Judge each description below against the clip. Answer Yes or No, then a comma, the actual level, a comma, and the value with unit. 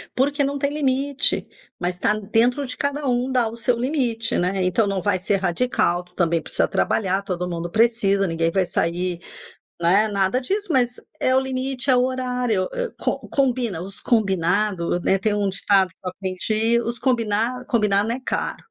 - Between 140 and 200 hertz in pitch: No, high, 220 Hz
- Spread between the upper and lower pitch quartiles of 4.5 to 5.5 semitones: Yes, average, 5.1 semitones